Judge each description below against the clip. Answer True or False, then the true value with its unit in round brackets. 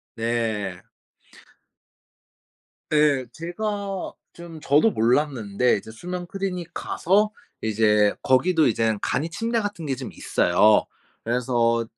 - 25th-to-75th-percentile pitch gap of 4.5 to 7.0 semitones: False (7.7 semitones)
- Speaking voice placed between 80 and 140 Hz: True (135 Hz)